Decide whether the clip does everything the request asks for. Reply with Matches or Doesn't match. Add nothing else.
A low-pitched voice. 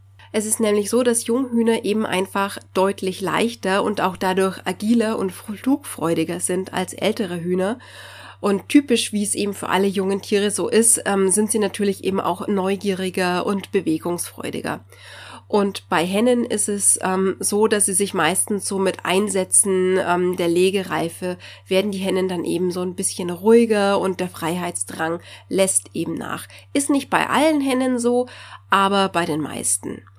Doesn't match